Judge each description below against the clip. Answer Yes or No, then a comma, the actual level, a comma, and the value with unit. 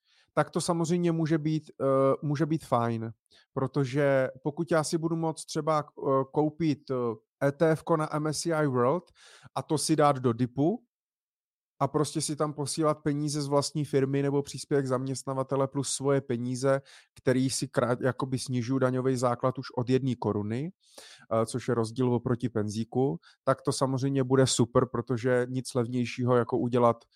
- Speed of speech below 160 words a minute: Yes, average, 145 wpm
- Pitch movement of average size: Yes, average, 3.2 semitones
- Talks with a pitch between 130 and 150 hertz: Yes, low, 135 Hz